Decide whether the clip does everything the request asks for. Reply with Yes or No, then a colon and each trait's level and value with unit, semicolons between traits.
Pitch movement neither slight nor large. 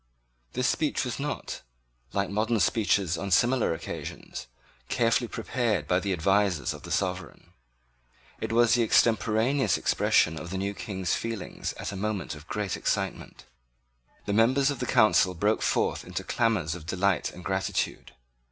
Yes: average, 4.1 semitones